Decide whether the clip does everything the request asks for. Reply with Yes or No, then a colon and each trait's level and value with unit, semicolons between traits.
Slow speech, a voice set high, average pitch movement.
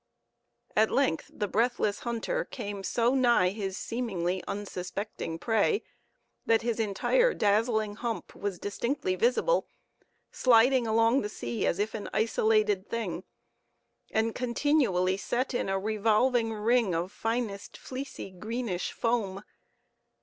Yes: slow, 120 wpm; high, 220 Hz; average, 3.3 semitones